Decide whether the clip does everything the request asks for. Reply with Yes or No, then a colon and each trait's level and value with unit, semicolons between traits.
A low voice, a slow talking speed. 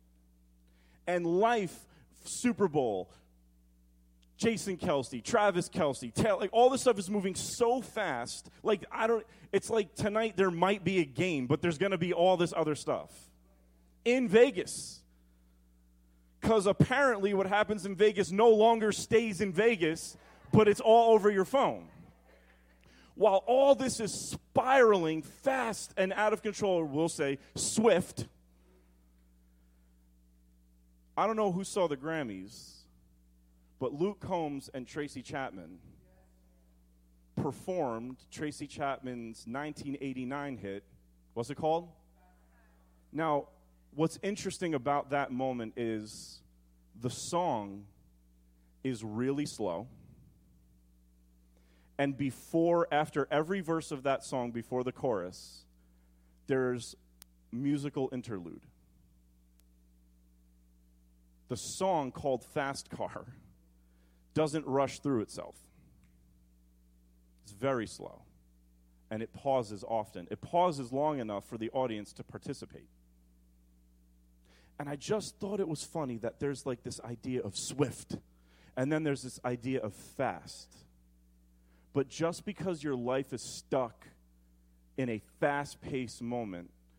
Yes: low, 125 Hz; slow, 120 wpm